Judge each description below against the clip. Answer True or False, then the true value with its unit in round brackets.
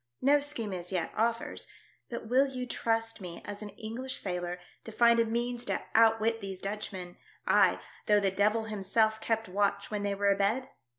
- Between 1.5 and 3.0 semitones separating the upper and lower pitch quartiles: True (2.7 semitones)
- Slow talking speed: False (180 wpm)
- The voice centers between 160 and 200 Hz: False (220 Hz)